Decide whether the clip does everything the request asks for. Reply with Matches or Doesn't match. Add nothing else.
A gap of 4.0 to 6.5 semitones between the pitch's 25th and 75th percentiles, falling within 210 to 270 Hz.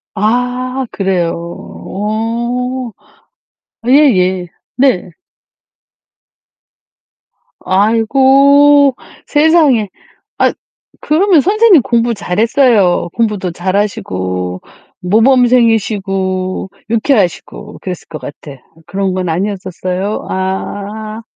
Matches